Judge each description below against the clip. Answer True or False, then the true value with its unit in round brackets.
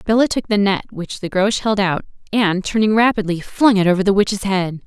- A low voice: False (200 Hz)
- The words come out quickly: True (220 wpm)